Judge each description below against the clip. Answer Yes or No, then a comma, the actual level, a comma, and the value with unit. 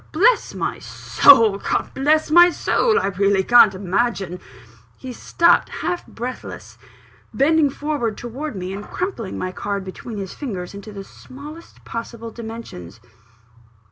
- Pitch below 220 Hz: No, high, 230 Hz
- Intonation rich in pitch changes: Yes, wide, 7.0 semitones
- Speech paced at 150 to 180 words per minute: No, average, 140 wpm